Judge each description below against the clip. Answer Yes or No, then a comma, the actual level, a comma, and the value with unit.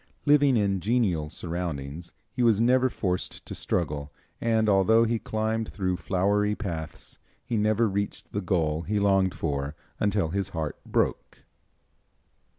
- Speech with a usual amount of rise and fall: Yes, average, 4.4 semitones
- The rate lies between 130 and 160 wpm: Yes, average, 140 wpm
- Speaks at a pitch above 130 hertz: No, low, 100 Hz